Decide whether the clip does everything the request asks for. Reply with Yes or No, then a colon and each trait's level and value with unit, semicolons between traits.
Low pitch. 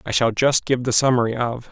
Yes: low, 120 Hz